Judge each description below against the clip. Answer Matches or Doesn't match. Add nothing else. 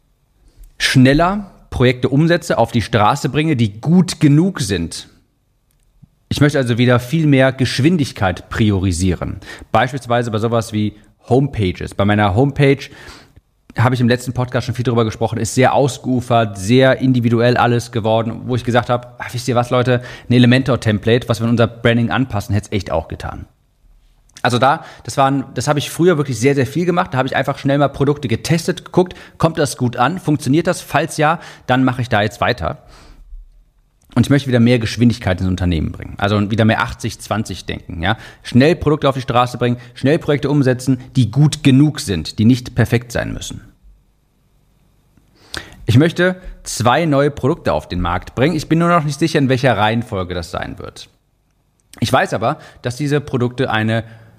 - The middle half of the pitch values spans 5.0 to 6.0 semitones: Doesn't match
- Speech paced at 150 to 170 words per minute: Doesn't match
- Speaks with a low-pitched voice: Matches